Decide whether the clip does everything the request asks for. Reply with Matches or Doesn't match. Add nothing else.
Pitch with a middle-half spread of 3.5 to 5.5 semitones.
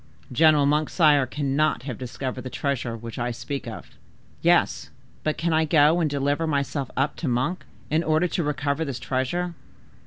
Doesn't match